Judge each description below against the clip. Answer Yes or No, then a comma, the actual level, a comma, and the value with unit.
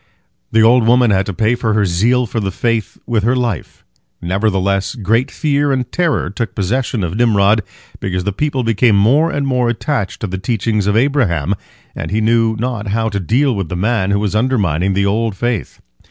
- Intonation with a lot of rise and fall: No, average, 3.7 semitones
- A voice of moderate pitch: No, low, 110 Hz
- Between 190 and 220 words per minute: Yes, average, 195 wpm